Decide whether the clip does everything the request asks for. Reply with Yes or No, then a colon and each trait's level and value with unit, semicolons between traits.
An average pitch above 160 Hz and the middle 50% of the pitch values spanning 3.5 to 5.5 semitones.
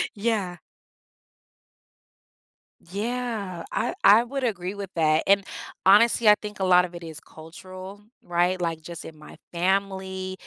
No: high, 190 Hz; average, 2.9 semitones